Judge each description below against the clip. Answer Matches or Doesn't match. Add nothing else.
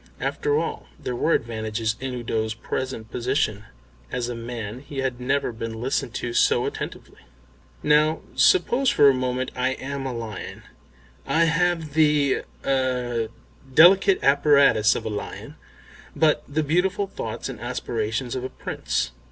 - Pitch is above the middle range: Doesn't match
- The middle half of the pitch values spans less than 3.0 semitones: Doesn't match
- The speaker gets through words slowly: Doesn't match